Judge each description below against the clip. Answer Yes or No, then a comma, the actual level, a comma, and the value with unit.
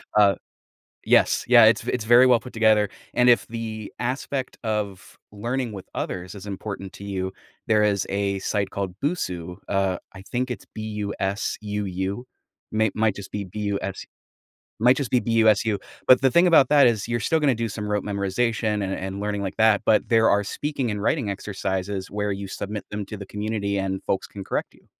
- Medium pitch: No, low, 105 Hz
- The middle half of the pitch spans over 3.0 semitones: No, narrow, 2.6 semitones